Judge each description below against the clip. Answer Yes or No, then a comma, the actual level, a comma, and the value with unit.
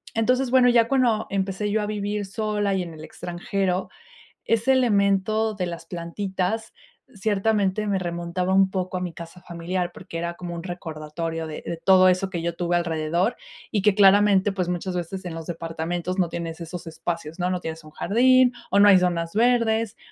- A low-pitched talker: No, medium, 185 Hz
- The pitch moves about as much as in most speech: Yes, average, 3.4 semitones